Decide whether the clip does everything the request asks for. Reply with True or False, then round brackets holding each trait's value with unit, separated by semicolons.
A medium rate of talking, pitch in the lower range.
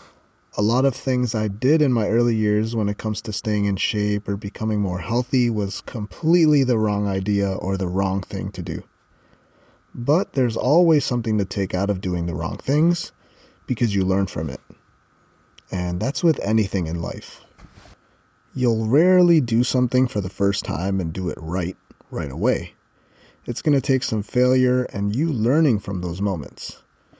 True (175 wpm; 105 Hz)